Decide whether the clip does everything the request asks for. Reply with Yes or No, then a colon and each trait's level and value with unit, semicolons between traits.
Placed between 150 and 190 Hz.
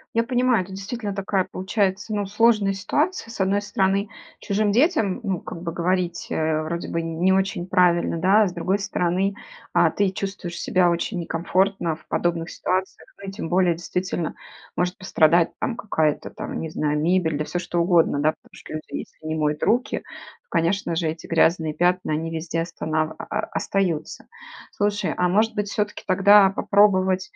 Yes: medium, 185 Hz